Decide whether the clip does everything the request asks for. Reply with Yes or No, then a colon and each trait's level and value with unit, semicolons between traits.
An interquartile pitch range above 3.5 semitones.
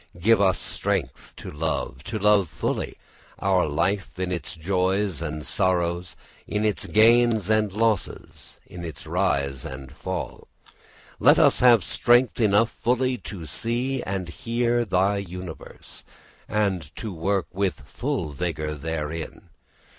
Yes: average, 4.7 semitones